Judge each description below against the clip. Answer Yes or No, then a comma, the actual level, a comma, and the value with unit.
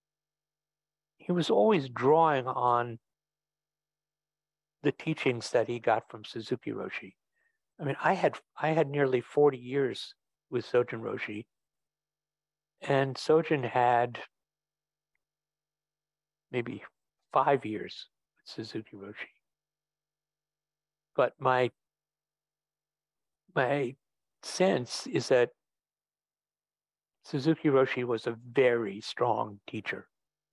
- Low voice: No, medium, 155 Hz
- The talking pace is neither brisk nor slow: No, slow, 90 wpm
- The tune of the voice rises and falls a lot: No, average, 3.2 semitones